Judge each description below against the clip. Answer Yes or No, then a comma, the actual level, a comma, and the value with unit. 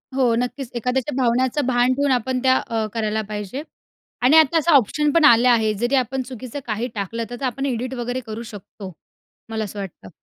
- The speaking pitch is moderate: No, high, 245 Hz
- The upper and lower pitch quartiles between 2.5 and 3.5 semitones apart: Yes, average, 2.9 semitones